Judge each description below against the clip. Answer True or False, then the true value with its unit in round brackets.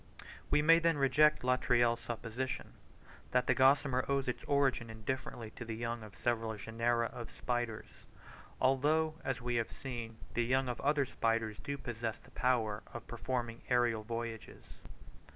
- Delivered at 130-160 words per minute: True (150 wpm)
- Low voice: True (120 Hz)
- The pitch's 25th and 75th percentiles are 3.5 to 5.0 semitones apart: False (2.5 semitones)